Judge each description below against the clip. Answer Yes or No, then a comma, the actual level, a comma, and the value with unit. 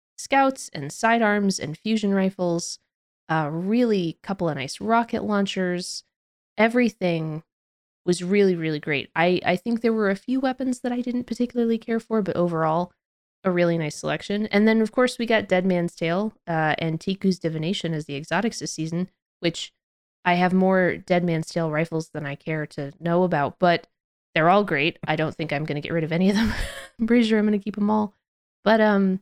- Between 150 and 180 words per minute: No, average, 195 wpm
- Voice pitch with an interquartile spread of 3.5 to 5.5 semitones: Yes, average, 5.0 semitones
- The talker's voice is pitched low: No, medium, 180 Hz